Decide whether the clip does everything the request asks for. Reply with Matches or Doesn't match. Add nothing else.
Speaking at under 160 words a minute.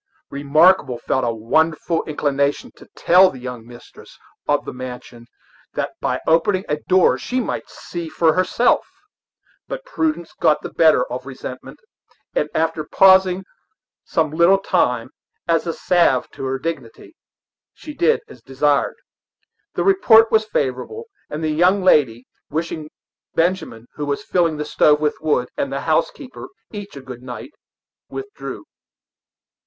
Matches